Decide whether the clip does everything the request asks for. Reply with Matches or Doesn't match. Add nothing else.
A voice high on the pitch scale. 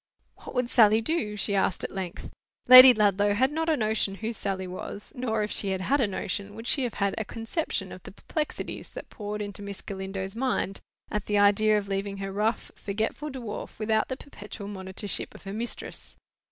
Matches